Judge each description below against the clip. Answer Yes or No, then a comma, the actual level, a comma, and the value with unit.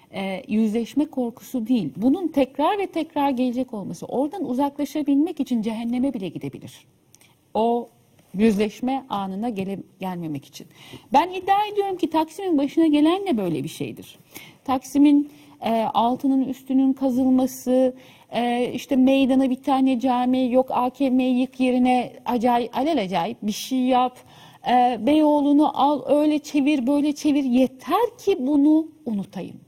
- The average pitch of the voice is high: Yes, very high, 260 Hz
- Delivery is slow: No, average, 130 wpm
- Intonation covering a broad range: No, average, 3.4 semitones